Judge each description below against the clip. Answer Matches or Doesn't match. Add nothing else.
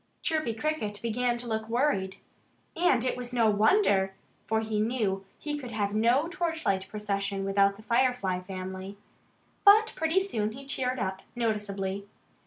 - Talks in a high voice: Matches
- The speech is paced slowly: Doesn't match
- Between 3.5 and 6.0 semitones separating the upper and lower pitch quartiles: Matches